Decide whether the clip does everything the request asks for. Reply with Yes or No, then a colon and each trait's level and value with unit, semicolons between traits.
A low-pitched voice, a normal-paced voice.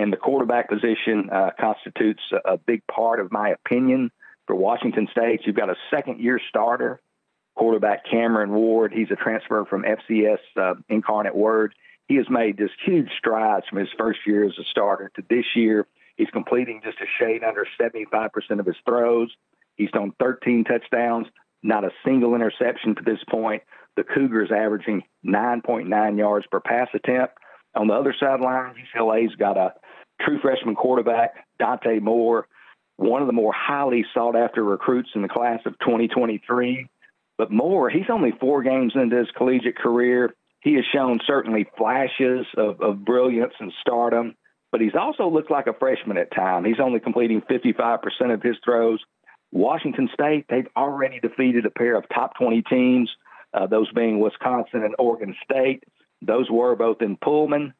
Yes: low, 115 Hz; average, 170 wpm